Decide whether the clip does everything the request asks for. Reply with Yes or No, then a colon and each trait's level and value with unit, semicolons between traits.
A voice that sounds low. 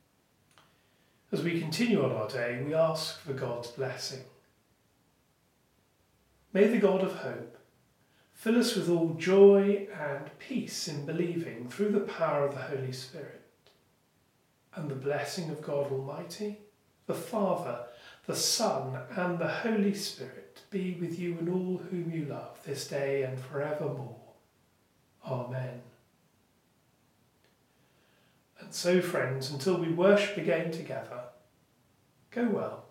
No: medium, 160 Hz